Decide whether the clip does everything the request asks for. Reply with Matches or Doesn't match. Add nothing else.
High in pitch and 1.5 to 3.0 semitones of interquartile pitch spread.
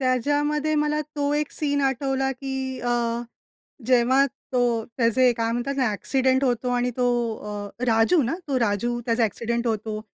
Matches